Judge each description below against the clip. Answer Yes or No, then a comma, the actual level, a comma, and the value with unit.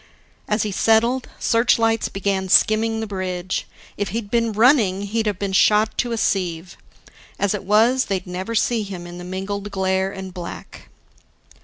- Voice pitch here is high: Yes, high, 205 Hz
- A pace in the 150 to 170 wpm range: Yes, average, 165 wpm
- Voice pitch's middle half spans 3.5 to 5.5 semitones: No, average, 3.0 semitones